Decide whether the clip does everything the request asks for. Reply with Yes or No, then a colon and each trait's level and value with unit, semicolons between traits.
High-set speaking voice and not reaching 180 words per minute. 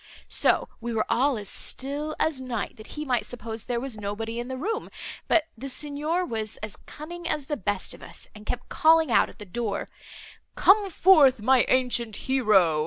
No: very high, 250 Hz; average, 190 wpm